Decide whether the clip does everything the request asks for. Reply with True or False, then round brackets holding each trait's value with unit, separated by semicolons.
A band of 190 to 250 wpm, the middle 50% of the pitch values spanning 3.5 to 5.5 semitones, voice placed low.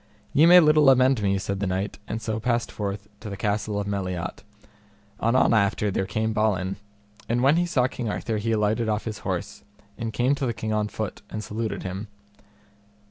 False (195 wpm; 2.8 semitones; 110 Hz)